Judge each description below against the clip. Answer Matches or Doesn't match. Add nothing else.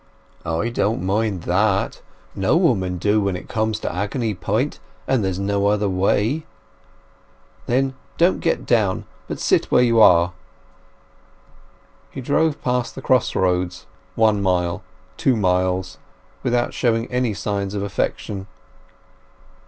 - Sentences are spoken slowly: Matches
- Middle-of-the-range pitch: Doesn't match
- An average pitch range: Matches